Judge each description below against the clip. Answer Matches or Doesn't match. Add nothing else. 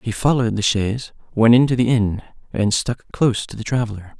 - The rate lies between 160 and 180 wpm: Doesn't match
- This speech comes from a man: Matches